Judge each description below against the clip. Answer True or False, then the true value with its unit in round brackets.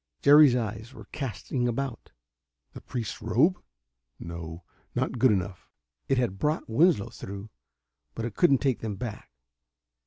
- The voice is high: False (120 Hz)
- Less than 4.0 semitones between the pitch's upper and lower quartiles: False (4.9 semitones)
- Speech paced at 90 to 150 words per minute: True (135 wpm)